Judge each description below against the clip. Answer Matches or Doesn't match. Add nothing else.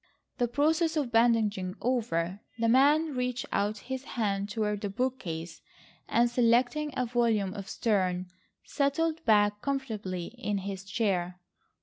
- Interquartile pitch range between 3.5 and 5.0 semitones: Matches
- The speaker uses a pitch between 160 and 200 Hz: Doesn't match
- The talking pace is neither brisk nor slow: Doesn't match